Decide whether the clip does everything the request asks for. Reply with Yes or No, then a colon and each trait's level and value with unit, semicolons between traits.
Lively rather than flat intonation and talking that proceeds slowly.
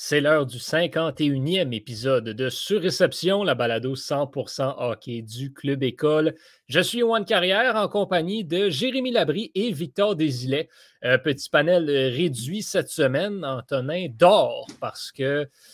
Yes: wide, 6.0 semitones; slow, 135 wpm